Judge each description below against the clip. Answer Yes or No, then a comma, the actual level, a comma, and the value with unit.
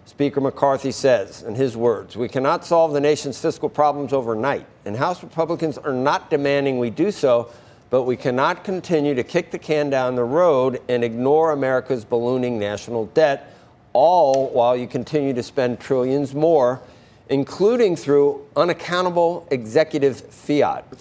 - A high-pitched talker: No, medium, 140 Hz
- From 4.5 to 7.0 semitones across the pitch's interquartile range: No, average, 3.5 semitones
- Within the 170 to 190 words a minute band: No, average, 150 wpm